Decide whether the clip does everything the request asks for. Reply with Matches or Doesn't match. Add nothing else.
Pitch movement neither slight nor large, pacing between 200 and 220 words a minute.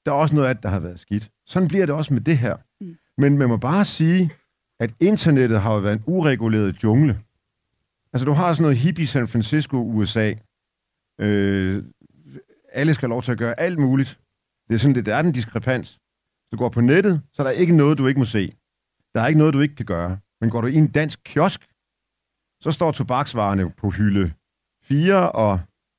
Doesn't match